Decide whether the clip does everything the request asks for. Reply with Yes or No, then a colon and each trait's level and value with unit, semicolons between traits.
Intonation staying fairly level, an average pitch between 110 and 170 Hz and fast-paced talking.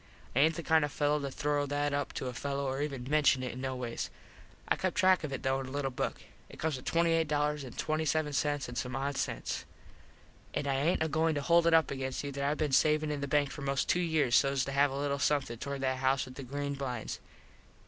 Yes: narrow, 2.0 semitones; medium, 140 Hz; fast, 245 wpm